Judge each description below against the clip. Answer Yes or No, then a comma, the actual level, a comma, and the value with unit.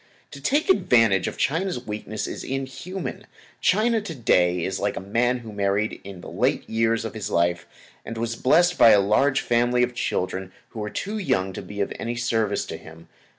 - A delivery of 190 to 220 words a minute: Yes, average, 195 wpm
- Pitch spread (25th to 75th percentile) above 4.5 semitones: Yes, average, 5.1 semitones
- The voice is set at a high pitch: No, low, 115 Hz